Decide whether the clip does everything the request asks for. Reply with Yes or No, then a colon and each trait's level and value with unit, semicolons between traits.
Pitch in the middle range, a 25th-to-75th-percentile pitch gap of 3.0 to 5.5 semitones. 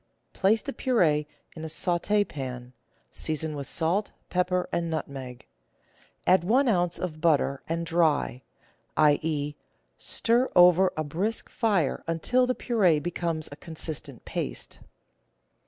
Yes: medium, 165 Hz; average, 3.8 semitones